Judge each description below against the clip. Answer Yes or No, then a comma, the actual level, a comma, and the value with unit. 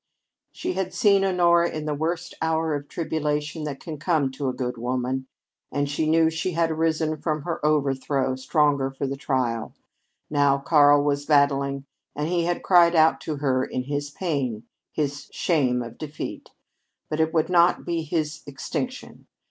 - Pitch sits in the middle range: Yes, medium, 150 Hz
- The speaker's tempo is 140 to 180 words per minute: Yes, average, 170 wpm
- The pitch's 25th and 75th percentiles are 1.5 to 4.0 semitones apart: Yes, average, 2.8 semitones